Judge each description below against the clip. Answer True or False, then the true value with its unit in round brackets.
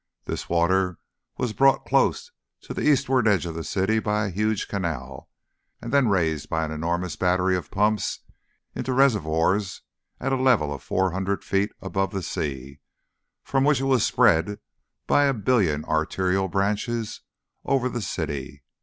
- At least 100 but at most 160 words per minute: True (155 wpm)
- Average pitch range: False (5.8 semitones)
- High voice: False (95 Hz)